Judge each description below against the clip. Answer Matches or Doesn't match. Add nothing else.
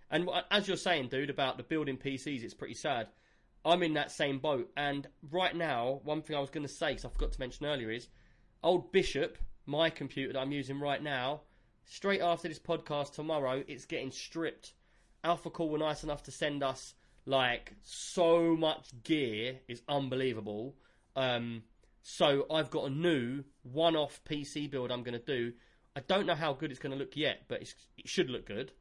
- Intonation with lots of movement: Doesn't match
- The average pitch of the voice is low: Doesn't match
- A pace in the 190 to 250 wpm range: Matches